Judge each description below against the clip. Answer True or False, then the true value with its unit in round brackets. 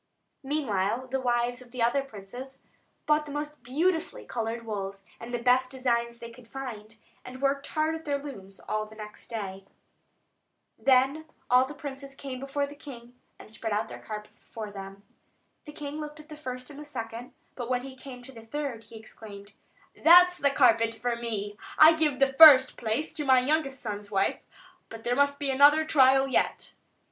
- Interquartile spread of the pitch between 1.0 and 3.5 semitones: False (3.9 semitones)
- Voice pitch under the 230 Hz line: False (255 Hz)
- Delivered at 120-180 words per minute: False (190 wpm)